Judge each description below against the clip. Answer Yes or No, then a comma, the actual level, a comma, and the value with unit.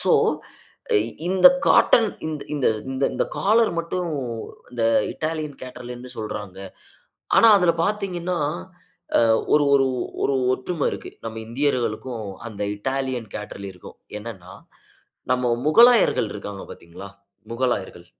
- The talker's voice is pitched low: Yes, low, 130 Hz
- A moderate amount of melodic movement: No, wide, 7.1 semitones